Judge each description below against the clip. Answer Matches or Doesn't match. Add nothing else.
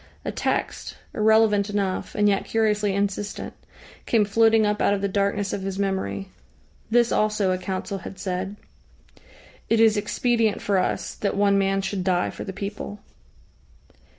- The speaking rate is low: Doesn't match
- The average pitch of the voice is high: Matches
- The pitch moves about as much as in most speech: Doesn't match